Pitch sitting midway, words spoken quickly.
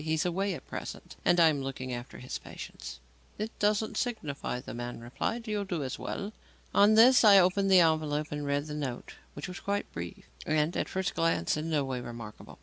Yes: medium, 155 Hz; fast, 210 wpm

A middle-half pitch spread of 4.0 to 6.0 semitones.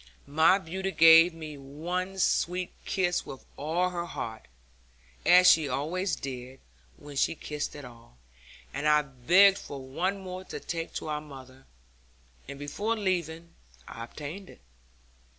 Yes: average, 4.5 semitones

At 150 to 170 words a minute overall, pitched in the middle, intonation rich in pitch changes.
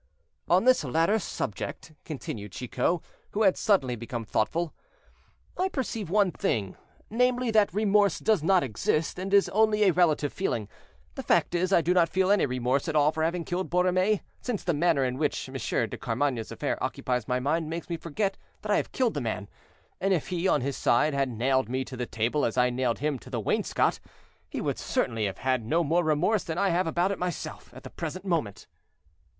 No: fast, 205 wpm; medium, 165 Hz; wide, 6.7 semitones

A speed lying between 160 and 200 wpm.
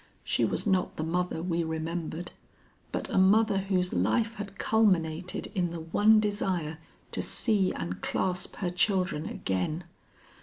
No: average, 145 wpm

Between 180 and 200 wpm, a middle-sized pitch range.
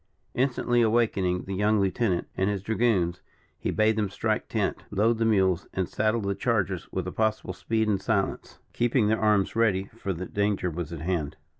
Yes: average, 185 wpm; average, 3.0 semitones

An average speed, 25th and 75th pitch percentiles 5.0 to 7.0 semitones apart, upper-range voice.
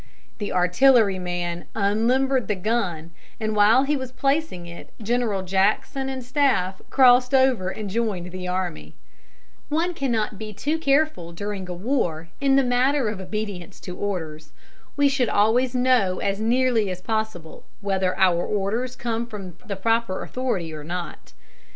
Yes: average, 150 wpm; wide, 5.6 semitones; high, 215 Hz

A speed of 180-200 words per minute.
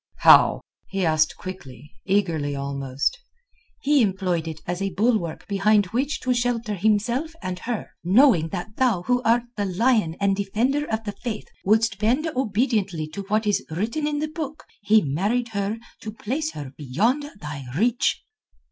No: average, 160 wpm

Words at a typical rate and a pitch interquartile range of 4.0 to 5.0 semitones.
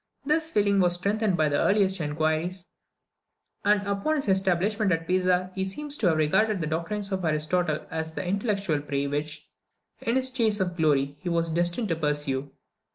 Yes: average, 175 wpm; average, 4.4 semitones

